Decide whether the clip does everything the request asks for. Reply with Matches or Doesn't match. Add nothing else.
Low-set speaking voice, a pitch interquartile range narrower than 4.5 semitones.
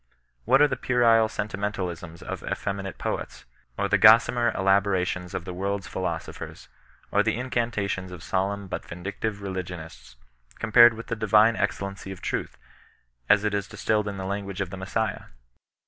Matches